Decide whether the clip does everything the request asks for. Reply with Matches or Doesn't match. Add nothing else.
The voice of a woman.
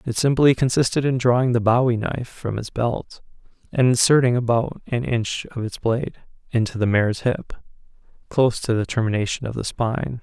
Doesn't match